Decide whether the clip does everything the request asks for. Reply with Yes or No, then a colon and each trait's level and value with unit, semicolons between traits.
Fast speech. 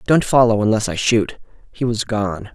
No: average, 190 wpm